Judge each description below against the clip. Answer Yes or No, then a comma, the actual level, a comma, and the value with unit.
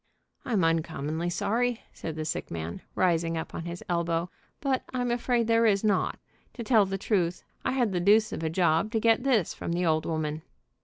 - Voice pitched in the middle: Yes, medium, 180 Hz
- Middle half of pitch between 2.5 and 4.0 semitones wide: No, wide, 5.5 semitones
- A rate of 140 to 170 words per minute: No, average, 200 wpm